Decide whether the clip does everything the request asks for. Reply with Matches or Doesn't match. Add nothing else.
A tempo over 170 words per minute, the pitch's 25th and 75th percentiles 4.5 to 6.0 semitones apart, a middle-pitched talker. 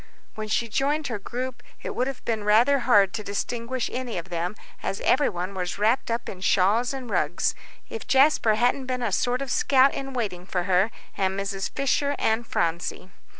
Doesn't match